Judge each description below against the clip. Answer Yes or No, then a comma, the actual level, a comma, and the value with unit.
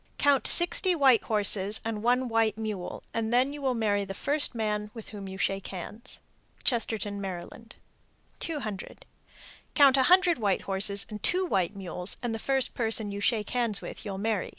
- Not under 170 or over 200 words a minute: Yes, average, 175 wpm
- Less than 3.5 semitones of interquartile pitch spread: No, average, 4.0 semitones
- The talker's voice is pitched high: Yes, high, 220 Hz